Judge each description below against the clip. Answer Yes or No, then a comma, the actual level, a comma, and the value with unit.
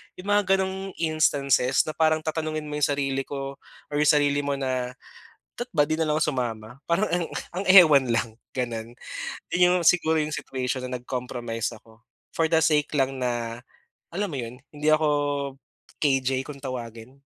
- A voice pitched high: No, medium, 140 Hz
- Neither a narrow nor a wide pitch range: Yes, average, 3.9 semitones